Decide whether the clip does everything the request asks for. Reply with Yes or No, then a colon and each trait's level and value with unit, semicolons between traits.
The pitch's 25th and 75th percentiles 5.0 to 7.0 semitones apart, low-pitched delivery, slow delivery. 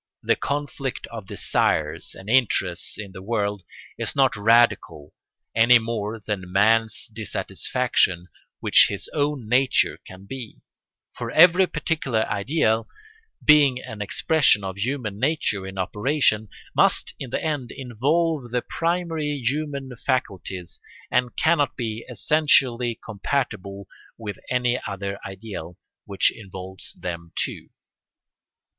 Yes: wide, 5.6 semitones; low, 115 Hz; slow, 120 wpm